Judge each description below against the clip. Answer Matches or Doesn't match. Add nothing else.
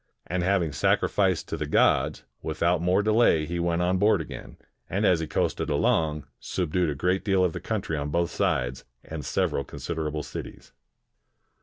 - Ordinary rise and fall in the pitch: Matches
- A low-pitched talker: Matches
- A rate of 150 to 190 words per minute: Matches